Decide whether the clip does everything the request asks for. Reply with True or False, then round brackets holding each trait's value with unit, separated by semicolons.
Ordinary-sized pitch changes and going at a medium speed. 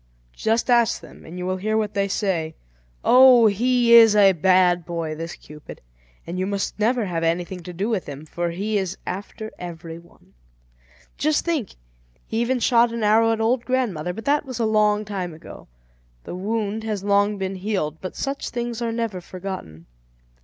True (4.3 semitones; 185 wpm)